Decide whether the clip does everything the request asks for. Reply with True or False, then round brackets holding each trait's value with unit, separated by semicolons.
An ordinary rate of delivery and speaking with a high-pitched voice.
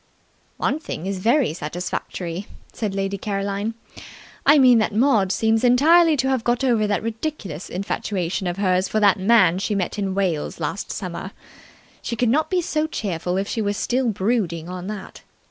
True (175 wpm; 205 Hz)